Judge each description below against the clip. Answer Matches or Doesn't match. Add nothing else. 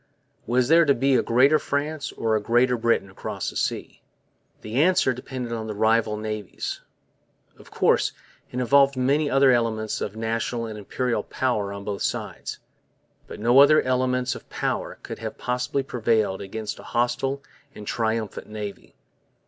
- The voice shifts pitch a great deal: Doesn't match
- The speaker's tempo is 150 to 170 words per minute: Matches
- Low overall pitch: Matches